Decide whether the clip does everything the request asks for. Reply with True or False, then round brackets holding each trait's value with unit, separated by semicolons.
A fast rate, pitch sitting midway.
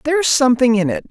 False (220 wpm; 260 Hz)